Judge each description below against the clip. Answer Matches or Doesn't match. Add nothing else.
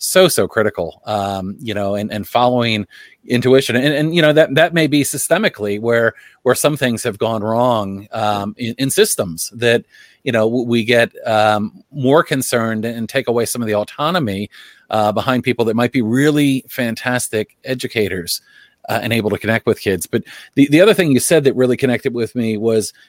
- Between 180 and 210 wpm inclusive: Matches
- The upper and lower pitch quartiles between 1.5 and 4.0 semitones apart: Matches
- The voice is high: Doesn't match